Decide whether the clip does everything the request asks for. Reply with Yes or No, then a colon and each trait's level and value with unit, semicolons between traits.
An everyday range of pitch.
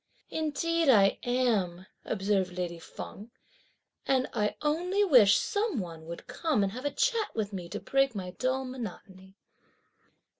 No: wide, 7.2 semitones